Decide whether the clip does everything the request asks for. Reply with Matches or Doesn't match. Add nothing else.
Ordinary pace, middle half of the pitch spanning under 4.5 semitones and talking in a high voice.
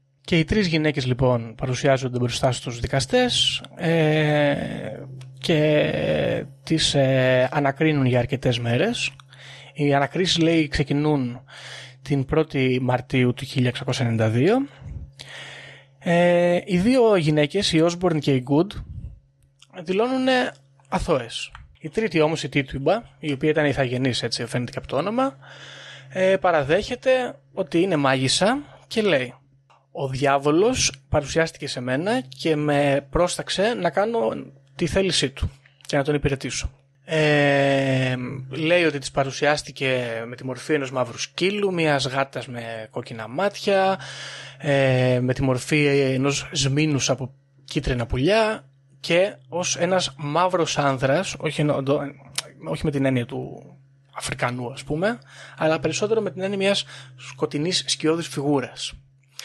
Doesn't match